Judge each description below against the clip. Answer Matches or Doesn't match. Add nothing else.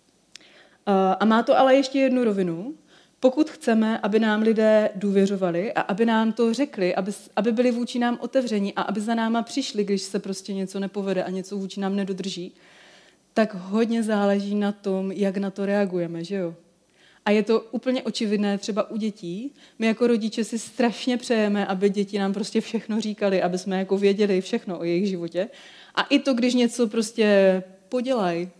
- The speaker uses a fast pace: Matches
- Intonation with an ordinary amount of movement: Matches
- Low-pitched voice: Doesn't match